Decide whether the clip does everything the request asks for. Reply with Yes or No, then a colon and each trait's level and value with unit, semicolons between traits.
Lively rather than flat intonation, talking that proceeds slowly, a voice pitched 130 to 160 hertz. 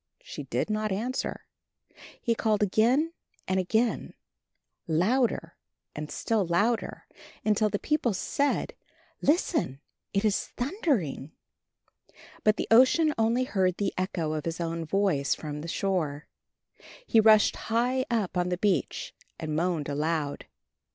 No: wide, 5.8 semitones; slow, 130 wpm; high, 205 Hz